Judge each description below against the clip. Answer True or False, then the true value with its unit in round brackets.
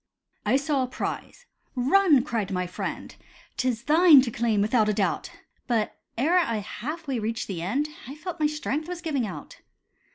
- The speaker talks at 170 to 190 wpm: True (175 wpm)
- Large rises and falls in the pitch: True (5.8 semitones)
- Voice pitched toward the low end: False (255 Hz)